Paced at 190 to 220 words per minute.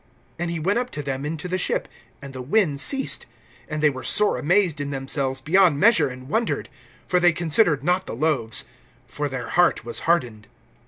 Yes: average, 195 wpm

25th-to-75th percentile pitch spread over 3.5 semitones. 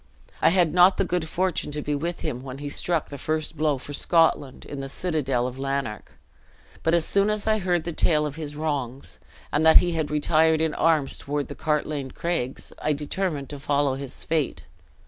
No: average, 2.8 semitones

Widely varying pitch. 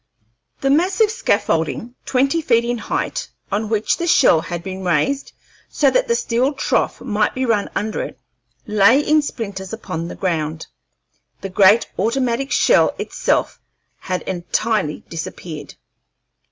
Yes: wide, 6.4 semitones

